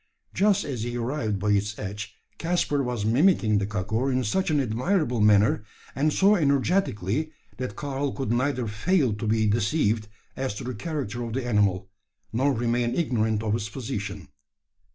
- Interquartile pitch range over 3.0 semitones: Yes, average, 5.1 semitones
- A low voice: Yes, low, 120 Hz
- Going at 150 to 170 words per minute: Yes, average, 165 wpm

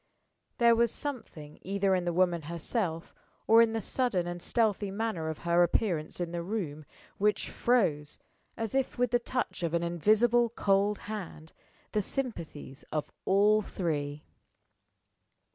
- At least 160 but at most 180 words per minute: No, average, 145 wpm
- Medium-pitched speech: No, high, 195 Hz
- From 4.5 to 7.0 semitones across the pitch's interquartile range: Yes, average, 5.1 semitones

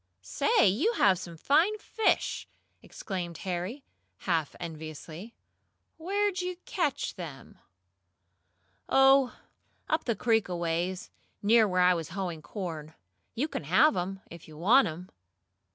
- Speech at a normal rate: No, slow, 125 wpm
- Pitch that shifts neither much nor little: No, wide, 7.9 semitones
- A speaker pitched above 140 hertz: Yes, high, 190 Hz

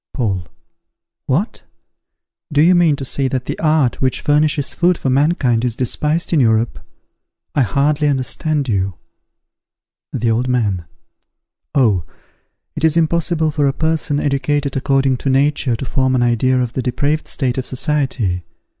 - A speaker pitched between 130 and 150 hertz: Yes, low, 135 Hz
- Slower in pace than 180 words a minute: Yes, average, 150 wpm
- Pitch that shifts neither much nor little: Yes, average, 3.4 semitones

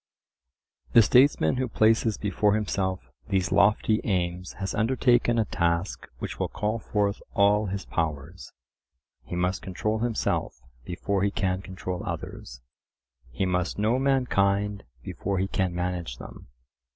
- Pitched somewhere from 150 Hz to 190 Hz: No, low, 100 Hz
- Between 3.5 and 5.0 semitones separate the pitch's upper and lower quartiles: No, average, 3.1 semitones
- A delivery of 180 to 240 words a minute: No, slow, 135 wpm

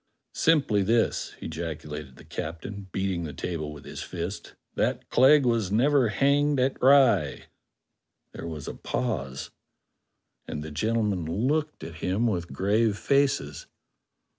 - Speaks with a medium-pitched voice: No, low, 100 Hz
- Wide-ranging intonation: Yes, wide, 7.6 semitones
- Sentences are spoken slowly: Yes, slow, 130 wpm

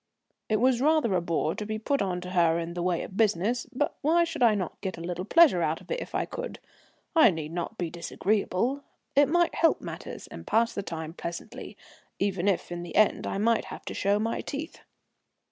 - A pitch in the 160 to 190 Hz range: No, high, 205 Hz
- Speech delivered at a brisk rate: Yes, fast, 220 wpm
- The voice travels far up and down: Yes, wide, 6.8 semitones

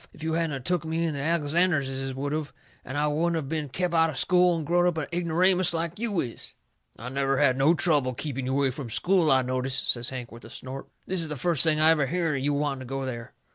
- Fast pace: Yes, fast, 260 wpm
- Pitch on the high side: No, medium, 150 Hz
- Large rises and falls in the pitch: No, average, 3.9 semitones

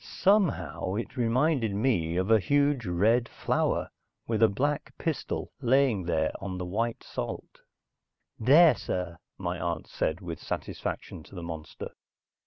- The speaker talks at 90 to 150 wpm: Yes, average, 140 wpm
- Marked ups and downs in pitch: Yes, wide, 6.8 semitones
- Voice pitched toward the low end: Yes, low, 110 Hz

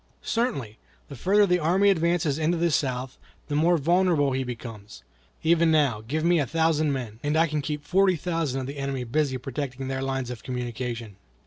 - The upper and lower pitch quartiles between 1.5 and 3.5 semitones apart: No, average, 4.3 semitones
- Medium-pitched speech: Yes, medium, 145 Hz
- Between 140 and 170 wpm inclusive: No, average, 190 wpm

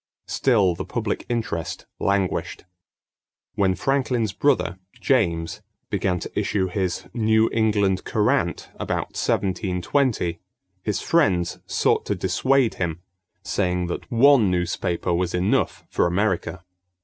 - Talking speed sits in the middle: No, slow, 115 wpm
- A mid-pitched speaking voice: No, very low, 95 Hz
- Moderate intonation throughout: Yes, average, 3.9 semitones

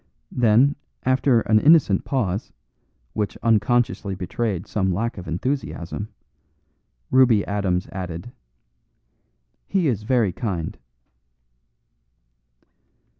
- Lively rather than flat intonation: No, average, 4.7 semitones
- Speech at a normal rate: No, slow, 85 wpm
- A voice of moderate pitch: No, low, 110 Hz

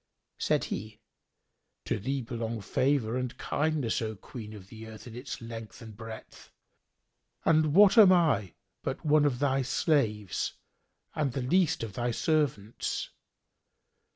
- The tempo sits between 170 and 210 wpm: No, average, 140 wpm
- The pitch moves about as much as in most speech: Yes, average, 4.9 semitones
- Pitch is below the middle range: Yes, low, 120 Hz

